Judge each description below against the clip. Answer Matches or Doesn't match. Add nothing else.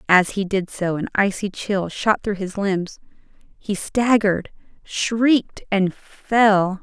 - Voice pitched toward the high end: Matches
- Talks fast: Doesn't match